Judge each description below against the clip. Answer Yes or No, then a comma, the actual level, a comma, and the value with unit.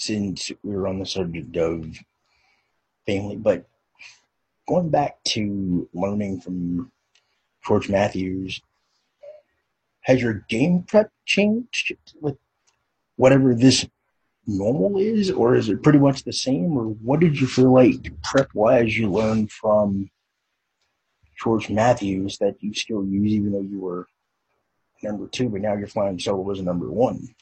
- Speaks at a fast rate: No, average, 140 wpm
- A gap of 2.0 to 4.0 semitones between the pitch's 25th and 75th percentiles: No, average, 5.3 semitones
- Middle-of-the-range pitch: No, low, 105 Hz